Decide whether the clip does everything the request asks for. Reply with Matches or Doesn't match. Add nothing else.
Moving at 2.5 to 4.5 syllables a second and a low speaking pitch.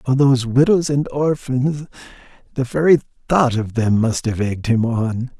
Matches